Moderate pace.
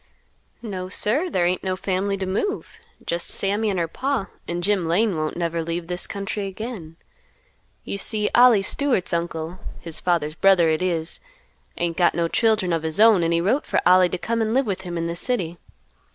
Yes: average, 195 wpm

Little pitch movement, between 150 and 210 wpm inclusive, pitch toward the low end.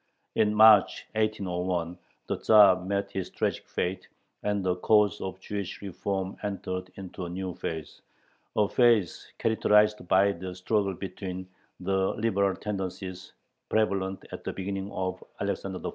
No: narrow, 2.0 semitones; average, 140 wpm; very low, 95 Hz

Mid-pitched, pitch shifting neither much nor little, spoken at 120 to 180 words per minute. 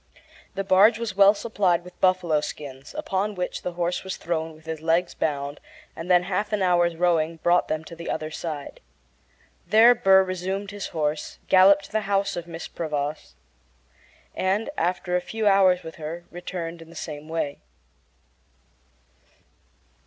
Yes: medium, 180 Hz; average, 3.1 semitones; average, 165 wpm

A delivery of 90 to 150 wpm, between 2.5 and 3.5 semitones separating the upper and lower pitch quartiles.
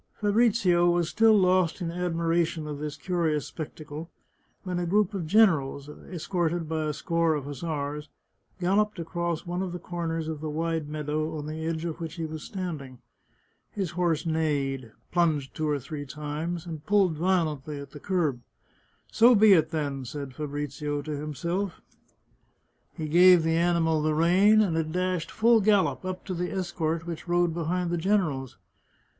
No: average, 175 wpm; average, 2.8 semitones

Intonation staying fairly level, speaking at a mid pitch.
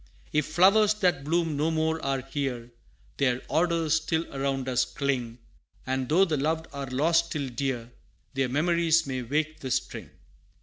No: average, 3.6 semitones; medium, 145 Hz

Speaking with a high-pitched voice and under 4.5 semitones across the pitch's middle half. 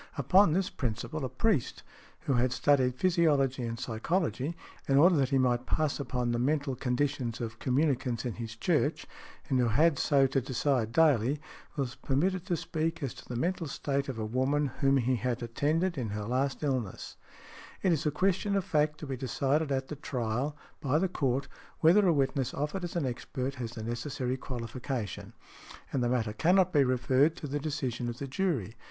No: low, 135 Hz; average, 3.8 semitones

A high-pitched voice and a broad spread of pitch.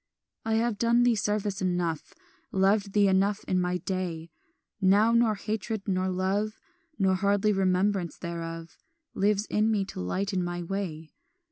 No: high, 195 Hz; narrow, 2.5 semitones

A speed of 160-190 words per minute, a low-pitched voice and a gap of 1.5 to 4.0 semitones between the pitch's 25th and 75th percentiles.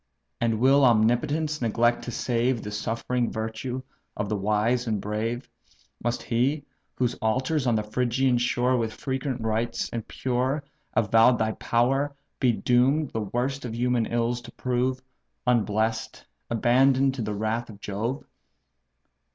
No: average, 145 wpm; low, 120 Hz; narrow, 2.5 semitones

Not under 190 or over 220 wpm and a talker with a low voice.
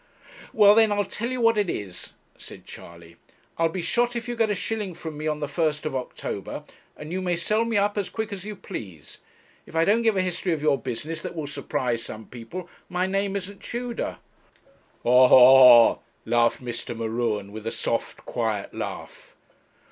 No: average, 195 wpm; medium, 165 Hz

